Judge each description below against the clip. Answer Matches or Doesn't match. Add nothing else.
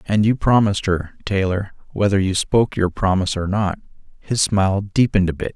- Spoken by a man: Matches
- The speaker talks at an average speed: Matches